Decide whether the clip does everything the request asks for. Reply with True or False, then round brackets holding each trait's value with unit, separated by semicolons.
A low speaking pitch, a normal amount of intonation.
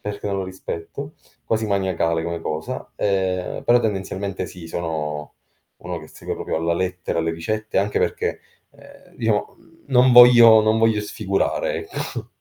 True (95 Hz; 4.5 semitones)